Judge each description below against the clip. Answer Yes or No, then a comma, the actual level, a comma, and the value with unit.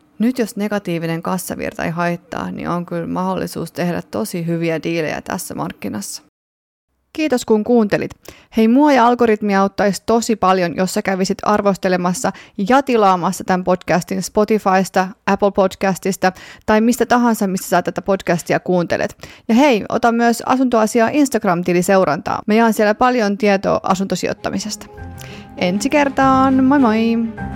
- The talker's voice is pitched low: No, high, 195 Hz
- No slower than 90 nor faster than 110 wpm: No, average, 135 wpm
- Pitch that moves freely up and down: No, average, 4.2 semitones